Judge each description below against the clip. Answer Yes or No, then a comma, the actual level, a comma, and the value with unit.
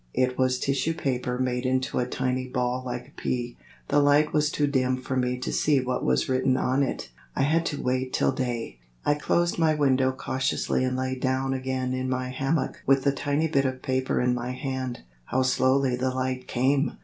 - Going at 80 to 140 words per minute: No, fast, 205 wpm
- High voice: No, low, 130 Hz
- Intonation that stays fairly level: Yes, narrow, 1.3 semitones